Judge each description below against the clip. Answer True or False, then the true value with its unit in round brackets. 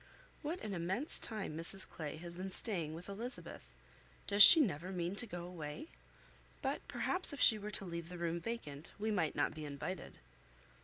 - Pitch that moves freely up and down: False (4.2 semitones)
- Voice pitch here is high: False (180 Hz)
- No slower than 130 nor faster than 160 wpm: False (185 wpm)